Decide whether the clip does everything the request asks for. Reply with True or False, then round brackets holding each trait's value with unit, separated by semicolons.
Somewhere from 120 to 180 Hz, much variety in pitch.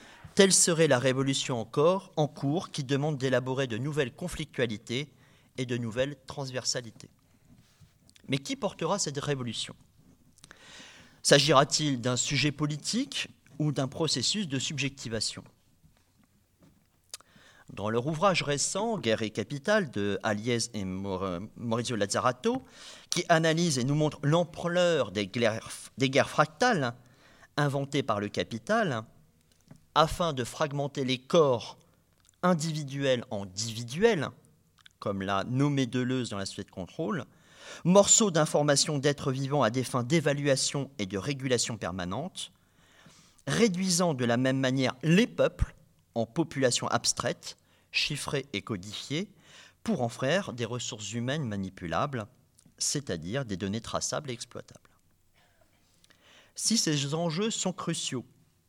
True (135 Hz; 5.7 semitones)